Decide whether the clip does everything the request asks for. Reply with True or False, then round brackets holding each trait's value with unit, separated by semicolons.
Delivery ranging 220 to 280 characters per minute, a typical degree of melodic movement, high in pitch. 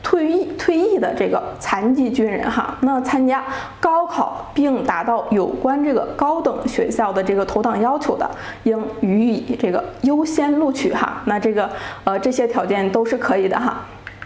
True (255 characters per minute; 4.9 semitones; 250 Hz)